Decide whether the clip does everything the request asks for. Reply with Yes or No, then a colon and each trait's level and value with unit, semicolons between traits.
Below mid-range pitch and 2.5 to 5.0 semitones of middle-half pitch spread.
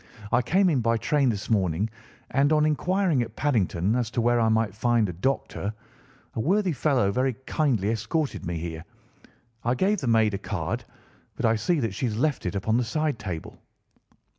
No: low, 115 Hz; wide, 5.6 semitones